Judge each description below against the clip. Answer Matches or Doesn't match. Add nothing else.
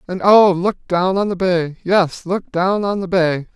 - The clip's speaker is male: Matches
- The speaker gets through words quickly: Matches